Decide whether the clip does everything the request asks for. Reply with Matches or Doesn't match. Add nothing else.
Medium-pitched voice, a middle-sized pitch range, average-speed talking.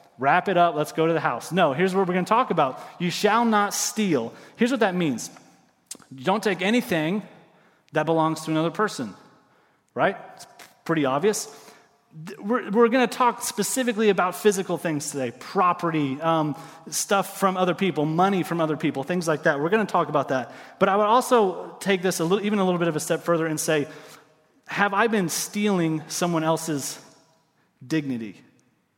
Matches